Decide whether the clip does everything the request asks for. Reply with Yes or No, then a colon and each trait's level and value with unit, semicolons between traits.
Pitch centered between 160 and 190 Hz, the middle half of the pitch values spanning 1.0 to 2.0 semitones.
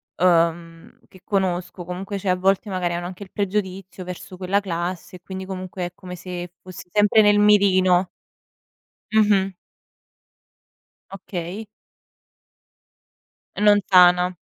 Yes: medium, 185 Hz; narrow, 1.7 semitones